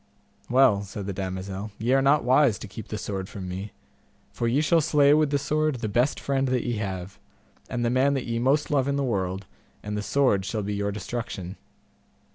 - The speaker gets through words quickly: Yes, fast, 215 wpm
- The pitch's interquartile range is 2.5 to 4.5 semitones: No, wide, 5.4 semitones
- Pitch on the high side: No, low, 115 Hz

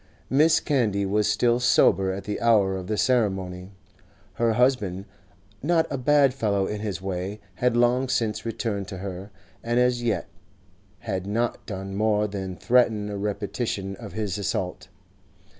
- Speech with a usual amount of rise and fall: Yes, average, 3.6 semitones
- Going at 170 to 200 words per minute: No, average, 155 wpm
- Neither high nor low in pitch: No, low, 105 Hz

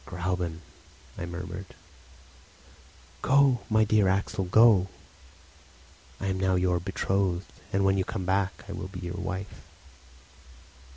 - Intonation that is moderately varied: No, narrow, 1.6 semitones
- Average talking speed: No, slow, 125 wpm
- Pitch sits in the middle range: No, very low, 95 Hz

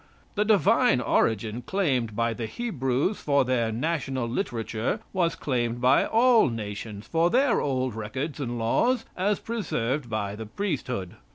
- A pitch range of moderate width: No, wide, 8.4 semitones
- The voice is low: Yes, low, 130 Hz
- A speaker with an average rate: Yes, average, 145 wpm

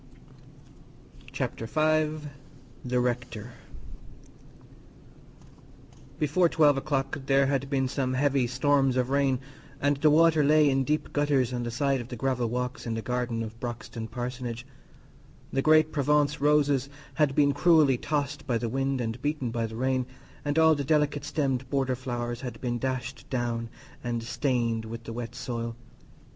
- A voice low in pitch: Yes, low, 130 Hz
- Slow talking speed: No, average, 155 wpm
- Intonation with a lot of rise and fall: No, average, 3.2 semitones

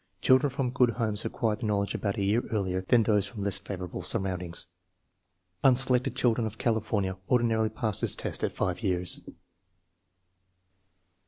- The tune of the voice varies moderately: Yes, average, 3.7 semitones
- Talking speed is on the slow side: No, average, 150 wpm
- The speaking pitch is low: Yes, low, 110 Hz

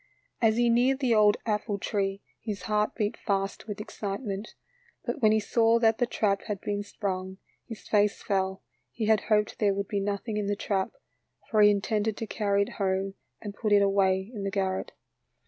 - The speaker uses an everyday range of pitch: No, narrow, 1.7 semitones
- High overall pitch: Yes, high, 205 Hz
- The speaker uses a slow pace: No, average, 195 wpm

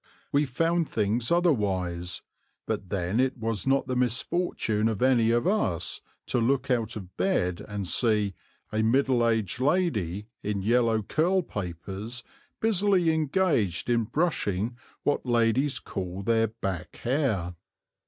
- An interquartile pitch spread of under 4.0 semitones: No, wide, 5.5 semitones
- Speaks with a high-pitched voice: No, low, 115 Hz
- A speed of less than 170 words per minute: Yes, slow, 135 wpm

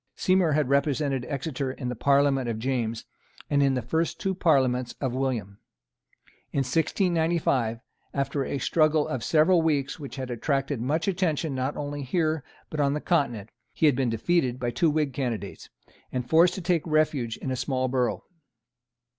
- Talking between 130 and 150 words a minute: No, average, 170 wpm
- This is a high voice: No, medium, 140 Hz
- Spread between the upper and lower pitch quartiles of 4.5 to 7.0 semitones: No, average, 3.6 semitones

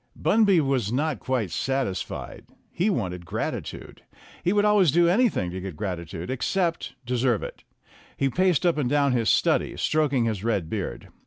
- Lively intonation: Yes, wide, 8.9 semitones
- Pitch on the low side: Yes, low, 130 Hz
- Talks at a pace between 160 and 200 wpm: Yes, average, 165 wpm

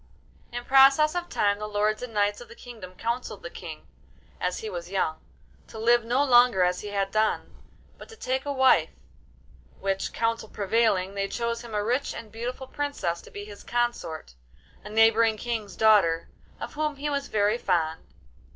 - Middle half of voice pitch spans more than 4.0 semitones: No, average, 3.6 semitones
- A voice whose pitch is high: Yes, high, 225 Hz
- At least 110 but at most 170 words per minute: No, average, 180 wpm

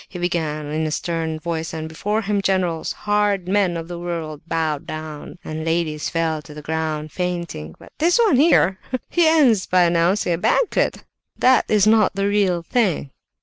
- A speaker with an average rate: Yes, average, 175 wpm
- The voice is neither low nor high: Yes, medium, 175 Hz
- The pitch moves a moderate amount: Yes, average, 4.3 semitones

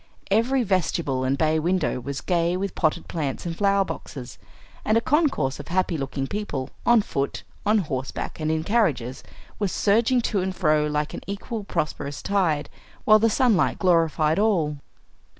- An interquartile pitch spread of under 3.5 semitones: No, wide, 5.5 semitones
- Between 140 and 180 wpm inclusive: Yes, average, 165 wpm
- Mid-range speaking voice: Yes, medium, 175 Hz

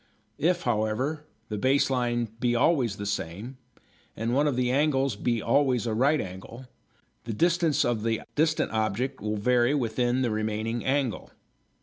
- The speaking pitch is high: No, low, 120 Hz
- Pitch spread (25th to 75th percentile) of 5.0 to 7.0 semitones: No, average, 3.9 semitones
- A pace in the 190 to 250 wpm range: No, average, 155 wpm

